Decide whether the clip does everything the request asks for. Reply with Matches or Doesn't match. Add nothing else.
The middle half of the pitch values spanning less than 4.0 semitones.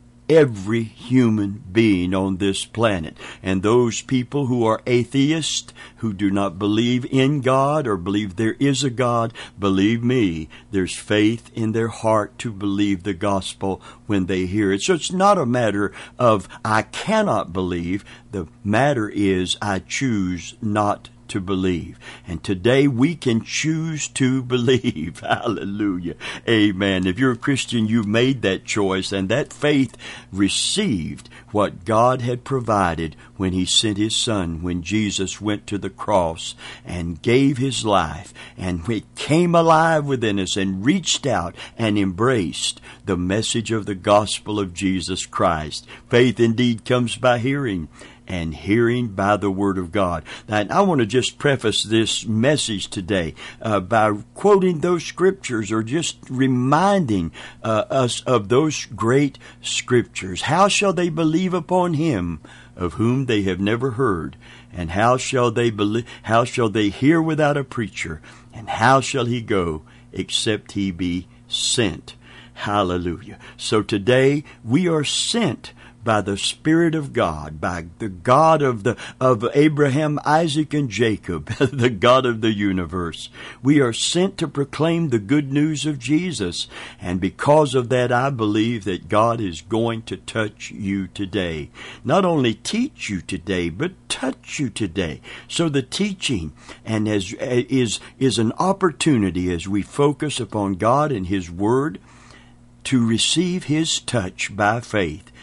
Doesn't match